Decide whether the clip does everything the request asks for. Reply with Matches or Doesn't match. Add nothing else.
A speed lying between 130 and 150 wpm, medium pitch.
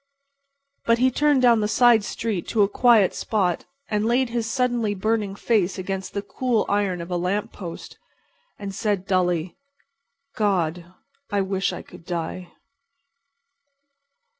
Doesn't match